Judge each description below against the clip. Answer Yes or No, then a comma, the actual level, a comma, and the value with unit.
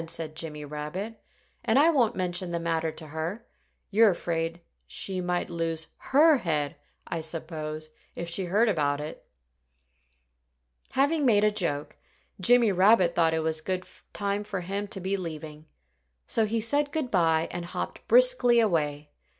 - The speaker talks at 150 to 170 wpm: Yes, average, 160 wpm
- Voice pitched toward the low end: No, medium, 175 Hz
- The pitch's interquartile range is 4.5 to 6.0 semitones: Yes, average, 5.0 semitones